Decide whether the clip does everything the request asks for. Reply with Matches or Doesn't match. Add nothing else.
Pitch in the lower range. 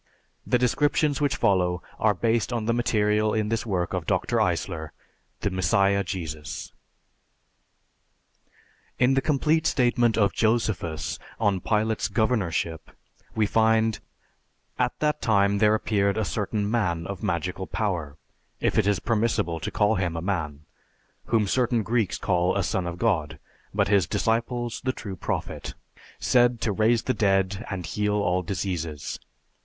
Matches